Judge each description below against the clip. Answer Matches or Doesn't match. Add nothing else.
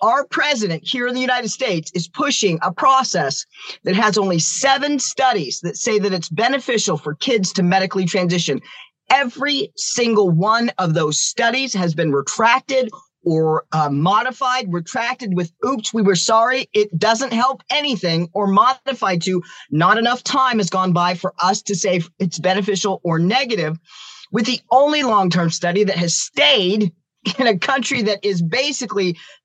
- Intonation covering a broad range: Matches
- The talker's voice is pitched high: Matches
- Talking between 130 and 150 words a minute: Doesn't match